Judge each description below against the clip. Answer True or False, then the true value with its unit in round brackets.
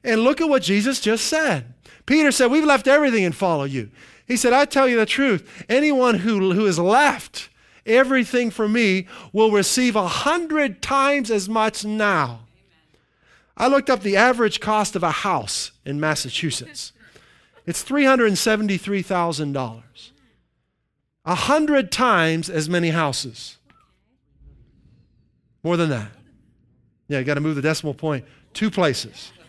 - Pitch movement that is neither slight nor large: False (8.8 semitones)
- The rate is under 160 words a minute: True (140 wpm)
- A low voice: False (200 Hz)